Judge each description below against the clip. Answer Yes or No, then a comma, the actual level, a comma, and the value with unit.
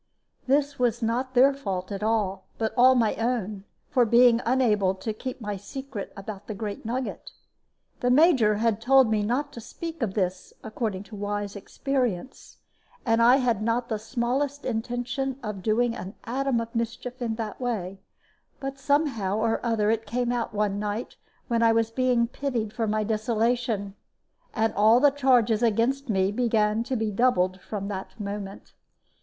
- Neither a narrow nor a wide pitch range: Yes, average, 3.1 semitones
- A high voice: Yes, high, 230 Hz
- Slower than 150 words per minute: No, average, 170 wpm